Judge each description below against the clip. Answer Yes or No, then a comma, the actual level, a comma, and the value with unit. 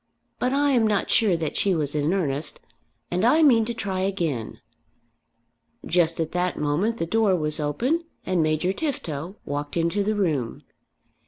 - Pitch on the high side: No, medium, 180 Hz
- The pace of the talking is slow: No, average, 165 wpm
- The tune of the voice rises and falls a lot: Yes, wide, 5.9 semitones